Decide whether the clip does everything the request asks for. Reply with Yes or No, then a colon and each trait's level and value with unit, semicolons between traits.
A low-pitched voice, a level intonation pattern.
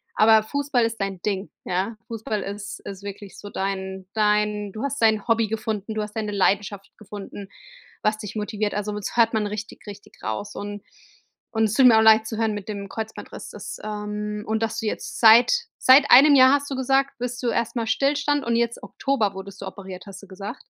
No: high, 215 Hz; narrow, 2.3 semitones